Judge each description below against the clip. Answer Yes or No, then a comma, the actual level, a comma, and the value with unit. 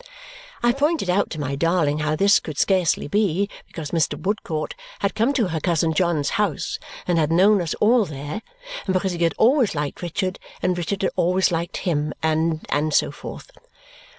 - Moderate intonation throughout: Yes, average, 4.3 semitones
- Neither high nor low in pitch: Yes, medium, 175 Hz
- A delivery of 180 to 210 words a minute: Yes, average, 185 wpm